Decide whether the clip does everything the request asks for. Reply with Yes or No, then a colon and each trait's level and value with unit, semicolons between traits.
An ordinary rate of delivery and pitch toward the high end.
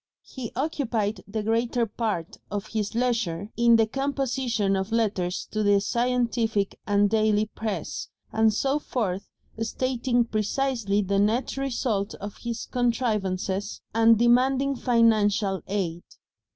No: slow, 125 wpm; high, 225 Hz